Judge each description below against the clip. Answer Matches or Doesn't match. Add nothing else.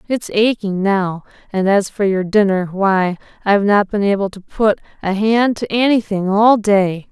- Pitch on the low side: Doesn't match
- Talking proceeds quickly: Doesn't match